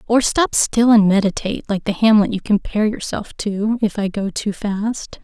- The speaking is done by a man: No, female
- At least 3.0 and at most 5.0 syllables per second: Yes, 4.8 syllables/s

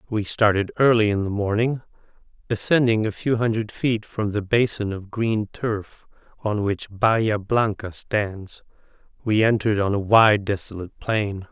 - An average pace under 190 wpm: Yes, average, 150 wpm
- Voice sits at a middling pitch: No, low, 105 Hz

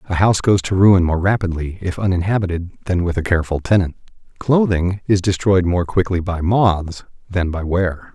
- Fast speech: No, average, 175 wpm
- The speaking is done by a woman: No, male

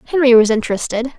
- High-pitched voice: Yes, high, 240 Hz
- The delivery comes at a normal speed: Yes, average, 150 wpm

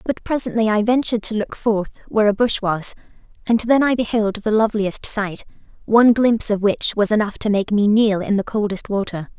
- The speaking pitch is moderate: No, high, 215 Hz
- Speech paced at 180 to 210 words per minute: Yes, average, 200 wpm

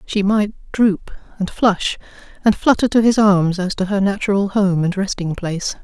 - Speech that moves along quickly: No, average, 185 wpm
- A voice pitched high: Yes, high, 200 Hz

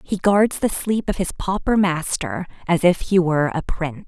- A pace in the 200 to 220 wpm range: Yes, fast, 205 wpm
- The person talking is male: No, female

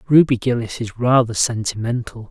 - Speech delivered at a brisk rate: No, slow, 130 wpm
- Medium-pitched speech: No, low, 120 Hz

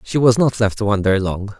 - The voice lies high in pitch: No, low, 105 Hz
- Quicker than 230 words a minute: Yes, fast, 265 wpm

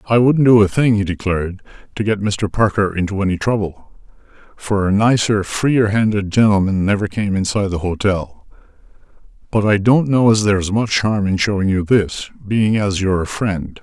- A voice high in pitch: No, low, 105 Hz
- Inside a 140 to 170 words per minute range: No, average, 180 wpm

